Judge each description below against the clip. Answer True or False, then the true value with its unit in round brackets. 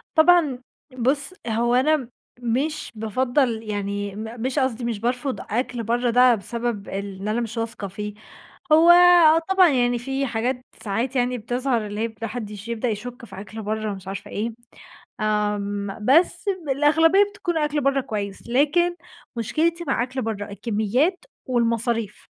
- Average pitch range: True (4.2 semitones)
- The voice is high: True (240 Hz)